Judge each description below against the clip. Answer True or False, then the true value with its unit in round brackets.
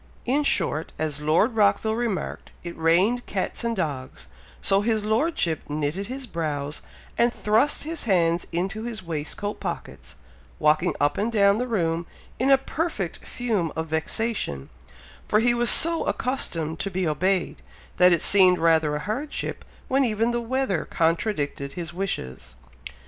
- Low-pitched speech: False (195 Hz)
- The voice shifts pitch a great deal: True (6.3 semitones)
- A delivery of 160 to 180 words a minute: False (150 wpm)